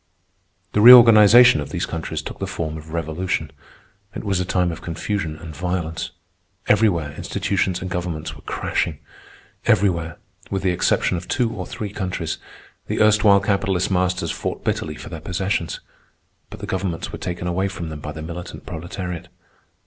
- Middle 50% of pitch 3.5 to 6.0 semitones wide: No, average, 3.0 semitones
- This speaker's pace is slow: No, average, 165 wpm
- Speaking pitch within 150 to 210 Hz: No, very low, 90 Hz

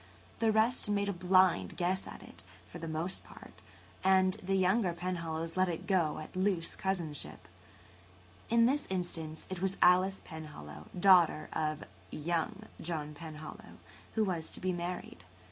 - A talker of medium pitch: Yes, medium, 180 Hz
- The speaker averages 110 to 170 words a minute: Yes, average, 160 wpm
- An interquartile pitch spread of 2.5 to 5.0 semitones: Yes, average, 3.1 semitones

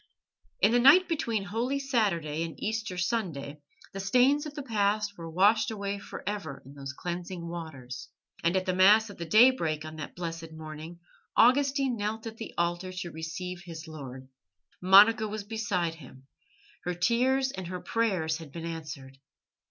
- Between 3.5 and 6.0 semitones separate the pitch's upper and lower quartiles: Yes, wide, 5.4 semitones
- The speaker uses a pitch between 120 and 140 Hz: No, medium, 185 Hz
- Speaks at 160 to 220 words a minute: Yes, average, 165 wpm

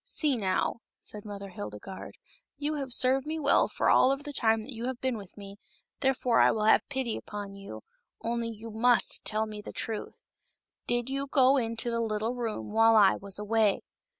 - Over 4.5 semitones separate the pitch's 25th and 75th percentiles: No, average, 3.7 semitones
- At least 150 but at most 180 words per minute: No, fast, 205 wpm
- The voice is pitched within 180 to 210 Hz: No, high, 225 Hz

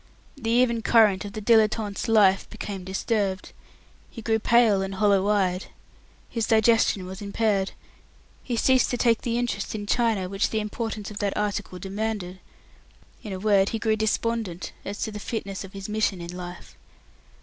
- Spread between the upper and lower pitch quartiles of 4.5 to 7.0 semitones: No, narrow, 2.5 semitones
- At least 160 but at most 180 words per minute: Yes, average, 170 wpm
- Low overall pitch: No, high, 210 Hz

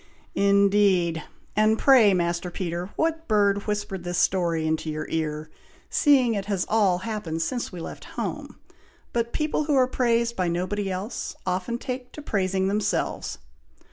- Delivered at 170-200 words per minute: No, average, 155 wpm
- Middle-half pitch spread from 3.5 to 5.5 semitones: Yes, average, 4.6 semitones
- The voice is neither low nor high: No, high, 200 Hz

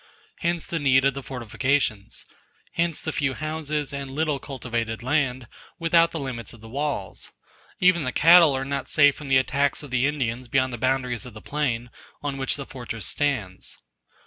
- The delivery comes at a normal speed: Yes, average, 180 wpm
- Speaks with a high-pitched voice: No, low, 135 Hz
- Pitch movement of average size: Yes, average, 3.1 semitones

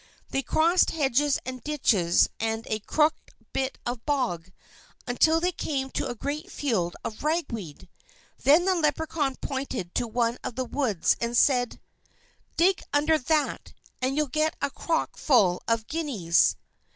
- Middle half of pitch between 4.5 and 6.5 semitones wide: Yes, average, 5.0 semitones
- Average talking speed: Yes, average, 150 wpm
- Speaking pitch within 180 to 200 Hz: No, very high, 270 Hz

